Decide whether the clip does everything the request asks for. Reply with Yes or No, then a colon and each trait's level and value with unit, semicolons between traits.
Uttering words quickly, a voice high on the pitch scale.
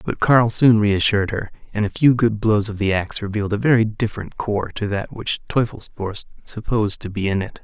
No: fast, 210 wpm; low, 105 Hz